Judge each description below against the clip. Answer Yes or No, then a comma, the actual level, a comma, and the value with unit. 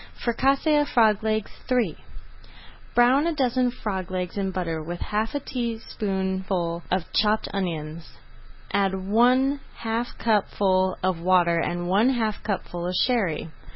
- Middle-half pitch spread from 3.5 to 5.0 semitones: Yes, average, 4.6 semitones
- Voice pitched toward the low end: No, high, 200 Hz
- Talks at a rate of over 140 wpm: No, slow, 135 wpm